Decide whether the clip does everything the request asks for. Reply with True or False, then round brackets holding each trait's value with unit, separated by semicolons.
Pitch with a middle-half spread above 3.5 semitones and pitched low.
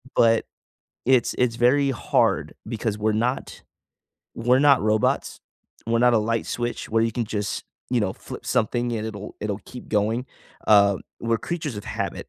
False (2.5 semitones; 115 Hz)